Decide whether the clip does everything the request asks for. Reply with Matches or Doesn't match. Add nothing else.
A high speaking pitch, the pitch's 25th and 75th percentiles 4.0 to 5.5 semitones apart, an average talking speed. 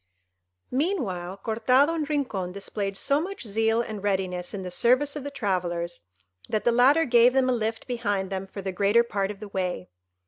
Matches